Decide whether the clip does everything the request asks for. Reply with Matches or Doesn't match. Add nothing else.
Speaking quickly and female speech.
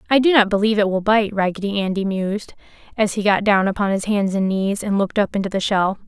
Matches